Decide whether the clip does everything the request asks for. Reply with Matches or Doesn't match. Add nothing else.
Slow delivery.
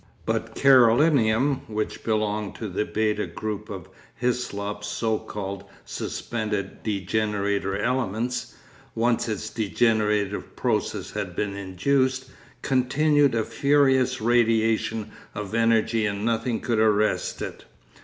Matches